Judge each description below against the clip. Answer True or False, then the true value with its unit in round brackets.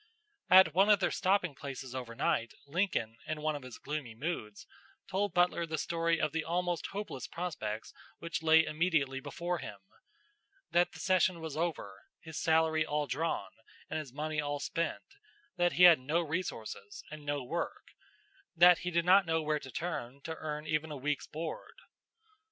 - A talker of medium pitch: True (160 Hz)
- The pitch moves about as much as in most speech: True (3.3 semitones)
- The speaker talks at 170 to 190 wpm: True (175 wpm)